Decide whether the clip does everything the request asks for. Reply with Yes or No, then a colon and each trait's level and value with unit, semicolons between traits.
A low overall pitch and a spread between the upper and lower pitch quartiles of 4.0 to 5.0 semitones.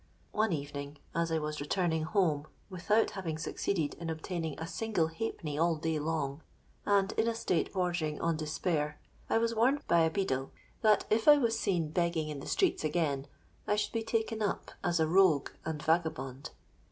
No: medium, 165 Hz; average, 4.7 semitones